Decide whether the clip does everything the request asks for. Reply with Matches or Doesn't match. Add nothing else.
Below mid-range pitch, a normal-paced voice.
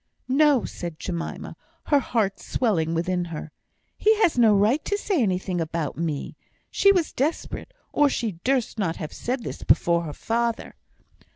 Doesn't match